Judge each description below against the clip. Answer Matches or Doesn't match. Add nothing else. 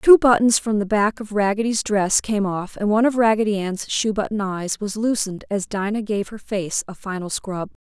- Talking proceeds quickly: Matches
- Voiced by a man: Doesn't match